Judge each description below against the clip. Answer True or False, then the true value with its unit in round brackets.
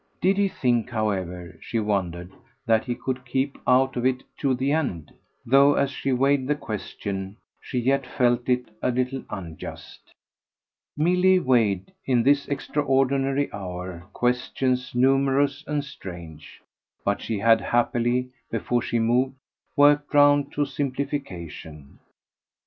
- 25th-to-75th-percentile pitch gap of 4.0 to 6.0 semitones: True (4.3 semitones)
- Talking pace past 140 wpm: False (135 wpm)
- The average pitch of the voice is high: False (125 Hz)